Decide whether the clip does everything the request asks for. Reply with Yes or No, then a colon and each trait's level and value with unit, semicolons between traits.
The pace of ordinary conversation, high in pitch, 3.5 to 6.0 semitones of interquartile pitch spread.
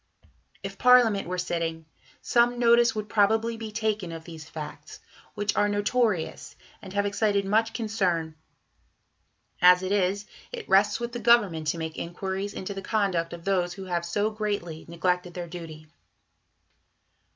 Yes: average, 150 wpm; high, 195 Hz; average, 4.1 semitones